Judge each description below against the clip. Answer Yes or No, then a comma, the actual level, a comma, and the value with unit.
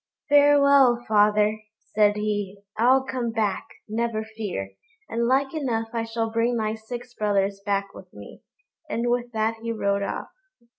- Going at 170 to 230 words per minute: No, average, 150 wpm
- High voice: Yes, high, 225 Hz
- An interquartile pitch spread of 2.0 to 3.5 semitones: Yes, narrow, 2.4 semitones